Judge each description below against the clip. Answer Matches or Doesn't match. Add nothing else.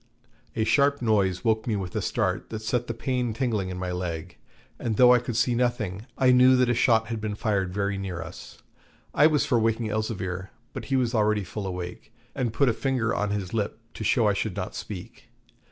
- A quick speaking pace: Matches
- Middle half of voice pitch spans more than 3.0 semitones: Matches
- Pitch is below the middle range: Matches